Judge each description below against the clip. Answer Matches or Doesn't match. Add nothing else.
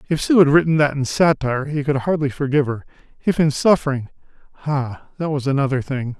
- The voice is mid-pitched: Matches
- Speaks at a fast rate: Doesn't match